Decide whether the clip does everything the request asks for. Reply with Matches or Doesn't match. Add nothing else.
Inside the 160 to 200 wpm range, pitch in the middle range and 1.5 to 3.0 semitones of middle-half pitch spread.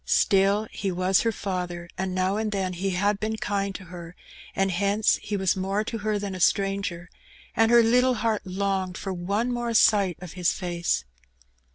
Doesn't match